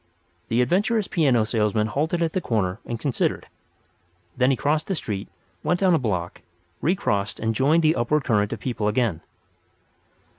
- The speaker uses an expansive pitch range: Yes, wide, 6.8 semitones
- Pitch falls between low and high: No, low, 125 Hz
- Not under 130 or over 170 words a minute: Yes, average, 160 wpm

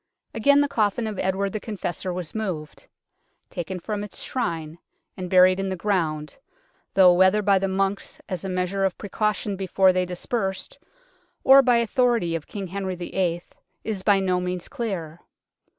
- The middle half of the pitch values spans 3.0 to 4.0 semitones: No, narrow, 2.6 semitones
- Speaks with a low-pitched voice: No, high, 190 Hz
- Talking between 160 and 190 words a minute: Yes, average, 165 wpm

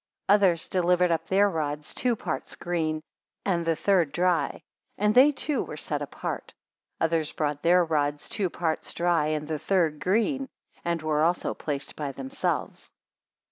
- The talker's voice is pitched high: No, medium, 170 Hz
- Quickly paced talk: No, average, 160 wpm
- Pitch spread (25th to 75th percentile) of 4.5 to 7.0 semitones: No, average, 3.3 semitones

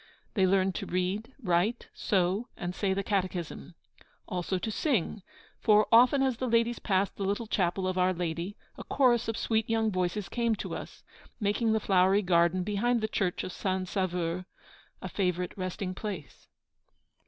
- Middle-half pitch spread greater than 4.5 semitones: No, average, 3.3 semitones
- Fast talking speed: No, average, 165 wpm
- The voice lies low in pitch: No, high, 195 Hz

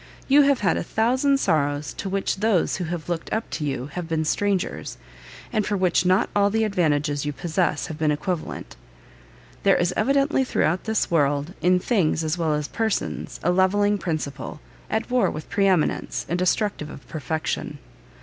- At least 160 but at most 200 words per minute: Yes, average, 180 wpm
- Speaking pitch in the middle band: Yes, medium, 180 Hz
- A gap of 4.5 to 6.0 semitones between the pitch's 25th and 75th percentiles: Yes, average, 4.8 semitones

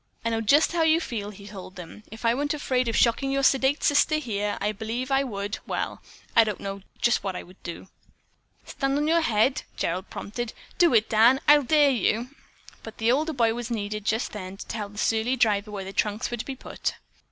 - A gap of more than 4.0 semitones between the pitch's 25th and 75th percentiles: Yes, average, 4.6 semitones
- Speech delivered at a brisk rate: Yes, fast, 220 wpm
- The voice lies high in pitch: Yes, high, 230 Hz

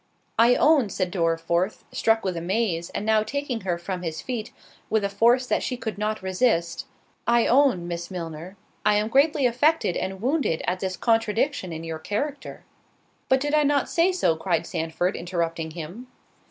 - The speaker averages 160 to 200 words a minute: Yes, average, 175 wpm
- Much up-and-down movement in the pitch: Yes, wide, 6.3 semitones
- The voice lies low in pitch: No, high, 205 Hz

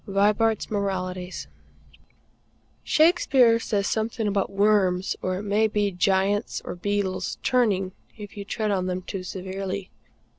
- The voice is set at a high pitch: Yes, high, 200 Hz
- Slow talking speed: Yes, slow, 125 wpm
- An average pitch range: No, narrow, 2.3 semitones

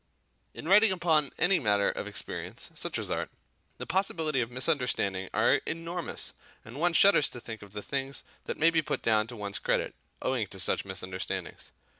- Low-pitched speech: Yes, low, 130 Hz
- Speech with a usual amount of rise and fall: No, wide, 7.9 semitones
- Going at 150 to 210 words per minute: Yes, average, 180 wpm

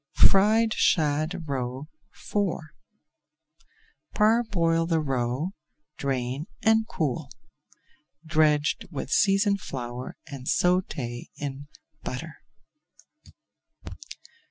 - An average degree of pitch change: No, wide, 5.8 semitones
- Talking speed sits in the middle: No, slow, 75 wpm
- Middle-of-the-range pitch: Yes, medium, 155 Hz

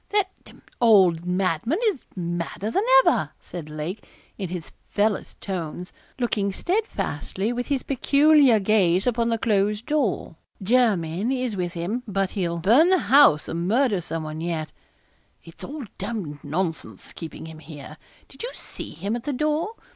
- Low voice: No, high, 200 Hz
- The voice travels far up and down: Yes, wide, 6.6 semitones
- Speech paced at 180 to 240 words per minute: No, average, 160 wpm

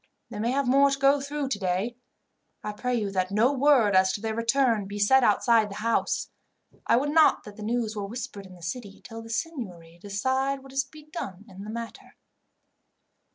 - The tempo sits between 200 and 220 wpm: Yes, fast, 205 wpm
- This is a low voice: No, high, 230 Hz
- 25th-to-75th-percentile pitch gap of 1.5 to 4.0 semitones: No, average, 4.8 semitones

